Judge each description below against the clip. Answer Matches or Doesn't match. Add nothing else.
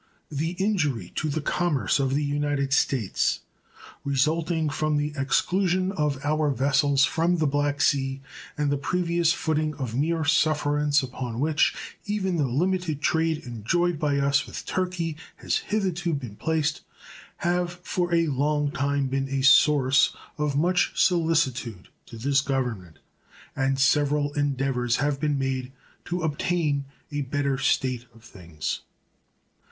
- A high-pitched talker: Doesn't match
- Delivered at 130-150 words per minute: Matches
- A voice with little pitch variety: Doesn't match